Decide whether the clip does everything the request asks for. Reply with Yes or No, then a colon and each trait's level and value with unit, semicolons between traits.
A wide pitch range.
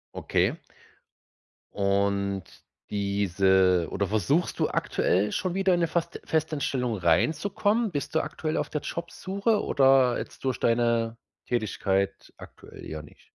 Yes: wide, 8.6 semitones